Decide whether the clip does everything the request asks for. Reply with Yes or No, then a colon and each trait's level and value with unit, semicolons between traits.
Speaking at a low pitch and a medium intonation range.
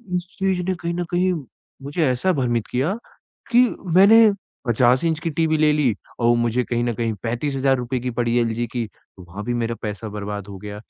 No: low, 125 Hz; wide, 5.8 semitones